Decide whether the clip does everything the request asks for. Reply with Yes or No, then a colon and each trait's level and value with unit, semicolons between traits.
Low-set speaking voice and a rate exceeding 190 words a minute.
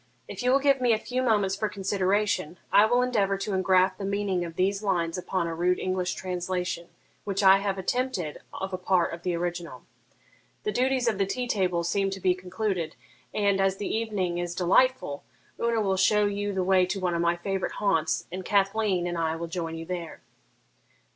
No: high, 190 Hz; average, 200 wpm